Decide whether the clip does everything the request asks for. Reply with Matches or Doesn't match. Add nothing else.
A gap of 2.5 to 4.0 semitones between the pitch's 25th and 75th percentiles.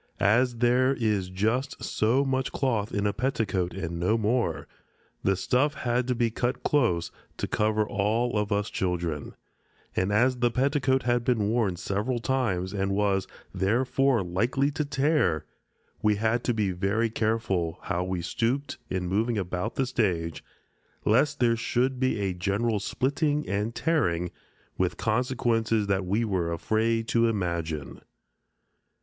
Doesn't match